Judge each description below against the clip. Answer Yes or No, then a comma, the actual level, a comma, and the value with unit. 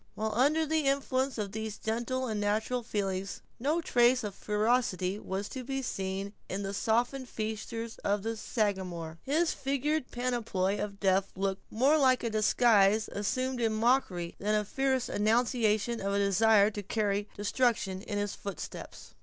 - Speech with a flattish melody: No, average, 3.8 semitones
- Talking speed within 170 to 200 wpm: No, average, 160 wpm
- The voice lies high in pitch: Yes, high, 220 Hz